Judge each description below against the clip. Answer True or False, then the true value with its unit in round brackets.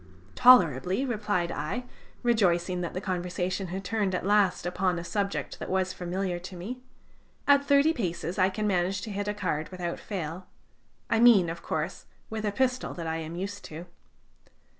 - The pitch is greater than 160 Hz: True (185 Hz)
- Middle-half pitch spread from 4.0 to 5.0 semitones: False (3.1 semitones)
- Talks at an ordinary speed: True (175 wpm)